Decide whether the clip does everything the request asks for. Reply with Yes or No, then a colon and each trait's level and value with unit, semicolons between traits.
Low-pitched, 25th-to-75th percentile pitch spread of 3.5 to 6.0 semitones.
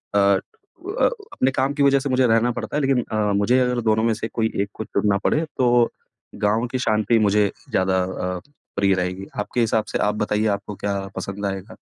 Yes: low, 110 Hz; average, 3.9 semitones